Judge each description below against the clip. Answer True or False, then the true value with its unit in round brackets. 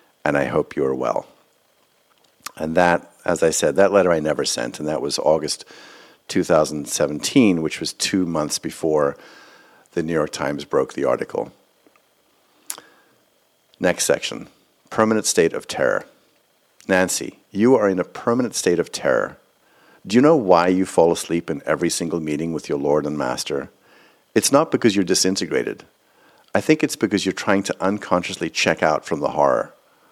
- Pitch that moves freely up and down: False (4.1 semitones)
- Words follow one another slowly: False (165 wpm)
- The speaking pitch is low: True (95 Hz)